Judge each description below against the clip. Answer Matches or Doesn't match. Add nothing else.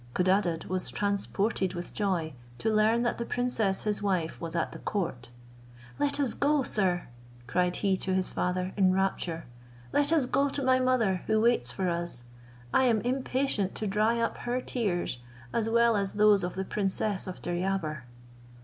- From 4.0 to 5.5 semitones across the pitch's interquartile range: Matches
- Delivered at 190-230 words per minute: Doesn't match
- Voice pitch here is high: Matches